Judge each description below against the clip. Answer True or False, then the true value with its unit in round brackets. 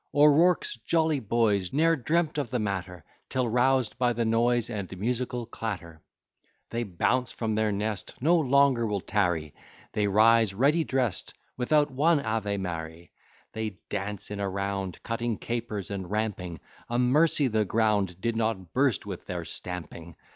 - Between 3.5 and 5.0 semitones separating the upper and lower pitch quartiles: True (4.3 semitones)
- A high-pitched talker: False (110 Hz)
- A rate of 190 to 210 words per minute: False (155 wpm)